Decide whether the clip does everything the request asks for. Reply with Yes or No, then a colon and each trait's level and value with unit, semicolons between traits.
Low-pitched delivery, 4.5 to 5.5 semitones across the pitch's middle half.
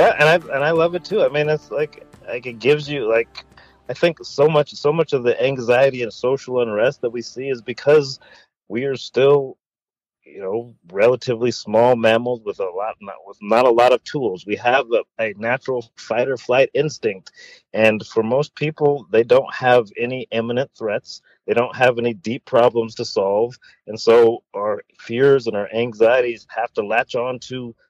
Yes: low, 130 Hz; average, 4.9 semitones